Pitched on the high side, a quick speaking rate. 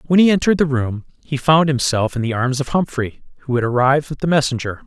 No: low, 135 Hz; fast, 235 wpm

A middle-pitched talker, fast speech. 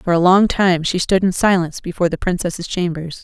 Yes: medium, 180 Hz; fast, 220 wpm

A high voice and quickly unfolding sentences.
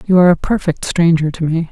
No: medium, 170 Hz; fast, 245 wpm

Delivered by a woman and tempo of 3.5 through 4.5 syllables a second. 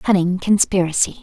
No: female; 6.1 syllables/s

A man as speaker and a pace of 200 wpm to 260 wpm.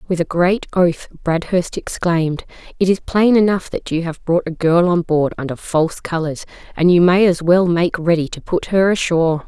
No: female; fast, 205 wpm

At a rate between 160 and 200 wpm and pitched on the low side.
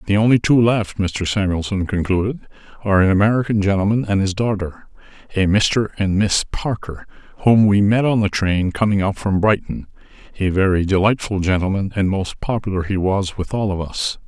Yes: average, 170 wpm; low, 100 Hz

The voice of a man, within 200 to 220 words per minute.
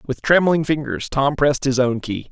Yes: male; fast, 205 wpm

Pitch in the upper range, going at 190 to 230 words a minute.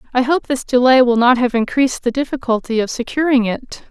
Yes: very high, 250 Hz; average, 200 wpm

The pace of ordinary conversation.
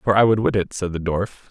No: fast, 320 wpm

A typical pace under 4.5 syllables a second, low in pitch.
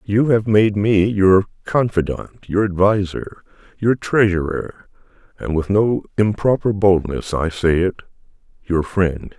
Yes: 4.0 syllables/s; low, 100 Hz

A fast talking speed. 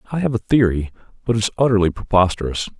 No: average, 195 wpm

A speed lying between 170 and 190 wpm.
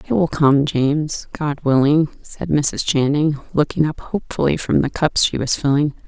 Yes: average, 180 wpm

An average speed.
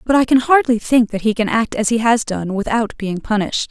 No: fast, 260 wpm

